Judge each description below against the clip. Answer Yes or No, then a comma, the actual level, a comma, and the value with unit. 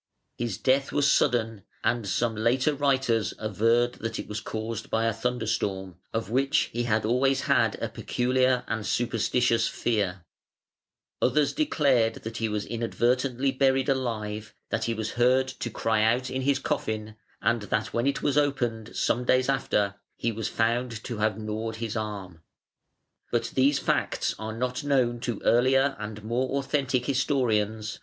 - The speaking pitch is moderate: No, low, 115 Hz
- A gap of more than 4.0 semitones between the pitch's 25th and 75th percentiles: No, average, 2.8 semitones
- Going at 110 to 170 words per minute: Yes, slow, 135 wpm